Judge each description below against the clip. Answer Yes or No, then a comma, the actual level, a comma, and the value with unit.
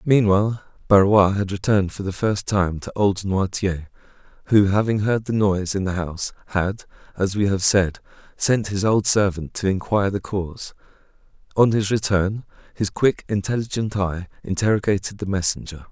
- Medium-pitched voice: No, low, 100 Hz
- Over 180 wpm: No, average, 160 wpm